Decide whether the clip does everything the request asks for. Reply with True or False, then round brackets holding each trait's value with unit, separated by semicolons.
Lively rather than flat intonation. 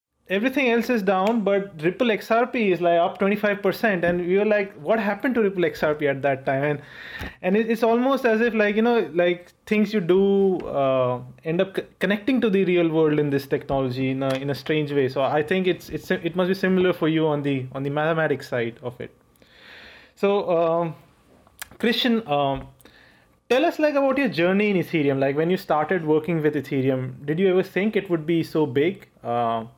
True (6.0 semitones)